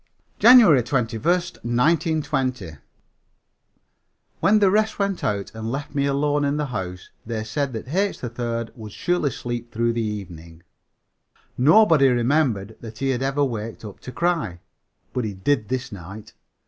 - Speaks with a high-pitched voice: No, low, 125 Hz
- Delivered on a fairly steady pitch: No, average, 5.1 semitones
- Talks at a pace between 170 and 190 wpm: No, average, 150 wpm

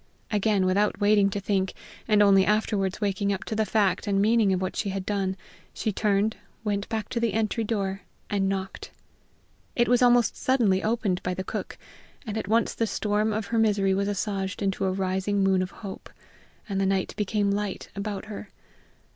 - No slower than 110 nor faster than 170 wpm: No, average, 190 wpm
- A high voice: Yes, high, 200 Hz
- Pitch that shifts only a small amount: Yes, narrow, 1.9 semitones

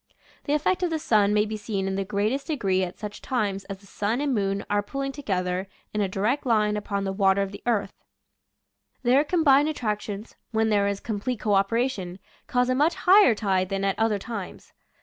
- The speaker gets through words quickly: Yes, fast, 210 wpm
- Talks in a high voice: Yes, high, 210 Hz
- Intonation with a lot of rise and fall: No, average, 4.3 semitones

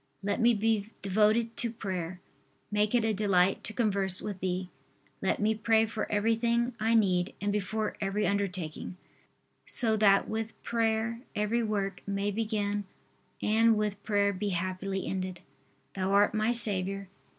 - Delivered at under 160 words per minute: Yes, average, 150 wpm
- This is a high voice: Yes, high, 210 Hz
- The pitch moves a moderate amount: No, narrow, 2.3 semitones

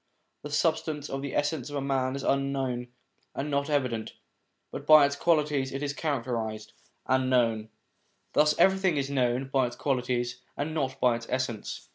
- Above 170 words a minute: No, average, 165 wpm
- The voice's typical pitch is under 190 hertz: Yes, low, 135 Hz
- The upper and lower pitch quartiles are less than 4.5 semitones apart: Yes, average, 2.8 semitones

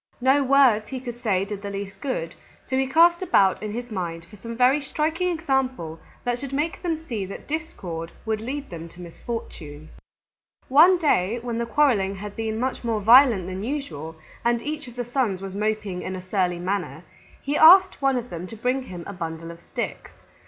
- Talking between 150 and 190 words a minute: No, average, 200 wpm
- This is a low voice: No, high, 230 Hz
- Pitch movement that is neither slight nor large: No, wide, 6.3 semitones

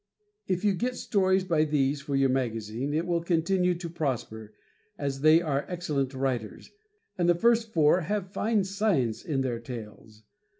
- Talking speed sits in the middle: Yes, average, 165 wpm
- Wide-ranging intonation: Yes, wide, 5.8 semitones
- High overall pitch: No, medium, 155 Hz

